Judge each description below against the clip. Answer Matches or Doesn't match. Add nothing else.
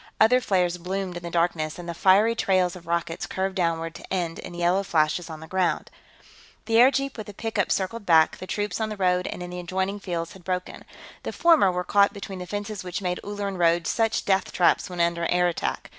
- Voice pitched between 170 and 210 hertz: Matches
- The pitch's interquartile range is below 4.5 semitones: Matches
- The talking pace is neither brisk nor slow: Doesn't match